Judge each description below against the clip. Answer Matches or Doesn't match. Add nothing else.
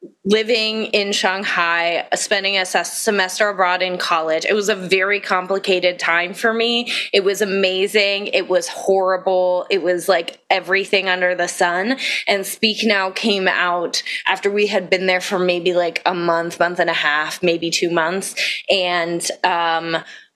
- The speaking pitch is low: Doesn't match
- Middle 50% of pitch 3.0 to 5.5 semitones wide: Doesn't match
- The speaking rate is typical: Matches